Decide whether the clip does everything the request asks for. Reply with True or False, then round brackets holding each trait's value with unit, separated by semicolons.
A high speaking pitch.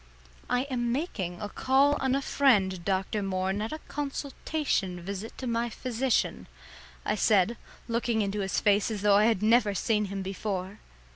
True (215 Hz)